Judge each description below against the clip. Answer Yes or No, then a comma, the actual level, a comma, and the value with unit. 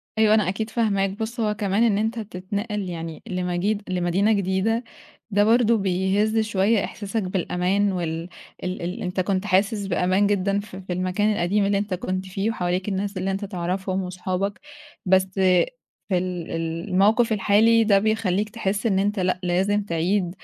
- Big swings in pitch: No, narrow, 2.4 semitones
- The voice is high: Yes, high, 195 Hz